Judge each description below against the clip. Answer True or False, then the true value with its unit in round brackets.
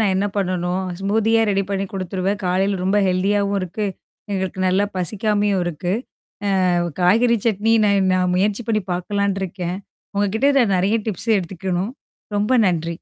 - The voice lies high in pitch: True (195 Hz)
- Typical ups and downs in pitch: False (2.0 semitones)